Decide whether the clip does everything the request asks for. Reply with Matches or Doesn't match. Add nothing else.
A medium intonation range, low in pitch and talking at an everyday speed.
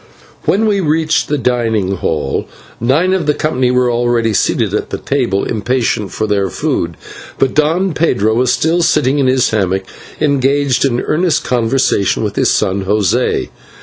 Doesn't match